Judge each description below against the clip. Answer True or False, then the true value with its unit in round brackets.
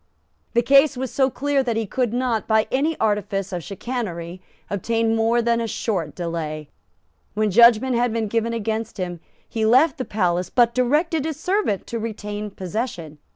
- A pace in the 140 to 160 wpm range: False (170 wpm)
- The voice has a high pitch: True (225 Hz)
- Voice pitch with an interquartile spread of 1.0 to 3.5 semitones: False (3.9 semitones)